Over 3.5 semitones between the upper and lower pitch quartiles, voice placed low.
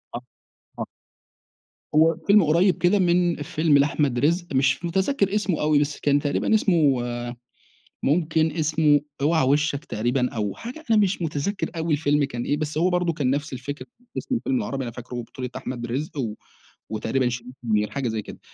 No: average, 4.7 semitones; medium, 150 Hz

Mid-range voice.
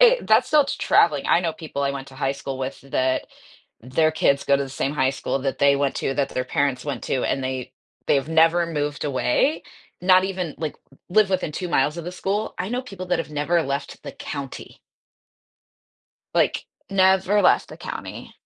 Yes: medium, 150 Hz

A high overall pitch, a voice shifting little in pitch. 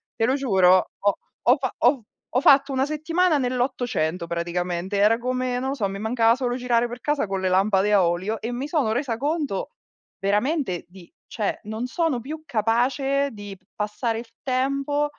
No: high, 240 Hz; average, 5.2 semitones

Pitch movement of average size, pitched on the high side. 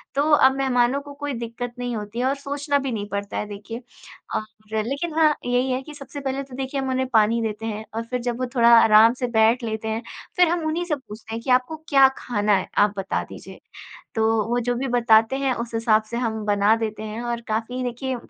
Yes: average, 3.3 semitones; high, 240 Hz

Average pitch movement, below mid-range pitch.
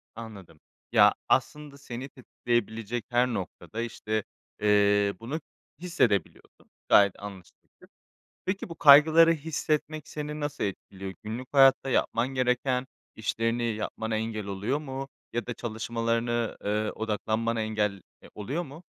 Yes: average, 4.3 semitones; low, 115 Hz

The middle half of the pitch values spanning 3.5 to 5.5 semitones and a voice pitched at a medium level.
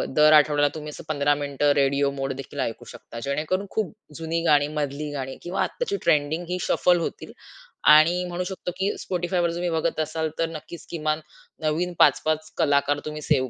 No: average, 3.0 semitones; medium, 155 Hz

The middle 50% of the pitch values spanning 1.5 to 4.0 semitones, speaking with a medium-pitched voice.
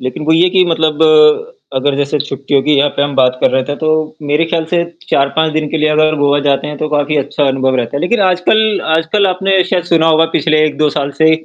Yes: narrow, 2.5 semitones; medium, 155 Hz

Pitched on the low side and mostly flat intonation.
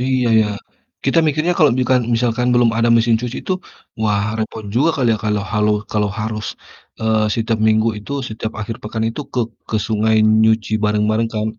Yes: low, 110 Hz; narrow, 2.2 semitones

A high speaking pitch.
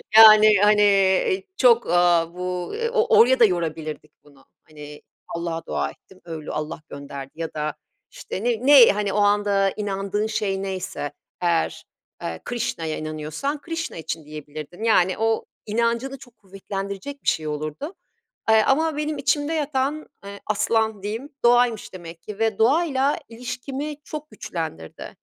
Yes: high, 205 Hz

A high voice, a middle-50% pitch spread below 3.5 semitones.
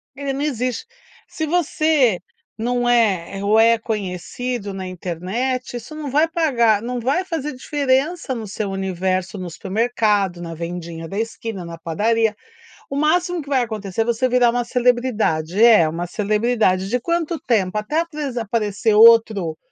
No: high, 230 Hz; average, 5.1 semitones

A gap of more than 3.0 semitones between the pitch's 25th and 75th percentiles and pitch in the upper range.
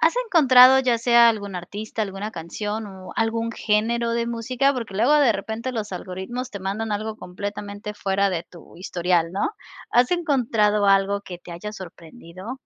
Yes: average, 3.5 semitones; high, 210 Hz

